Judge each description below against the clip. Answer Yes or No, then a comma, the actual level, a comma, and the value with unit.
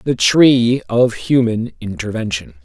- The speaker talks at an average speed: No, slow, 115 wpm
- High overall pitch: No, low, 110 Hz